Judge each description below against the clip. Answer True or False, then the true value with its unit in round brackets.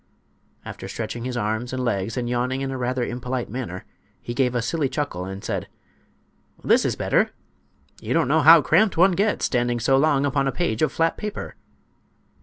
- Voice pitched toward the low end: True (130 Hz)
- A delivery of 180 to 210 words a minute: True (190 wpm)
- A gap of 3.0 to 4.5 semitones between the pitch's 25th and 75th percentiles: True (3.6 semitones)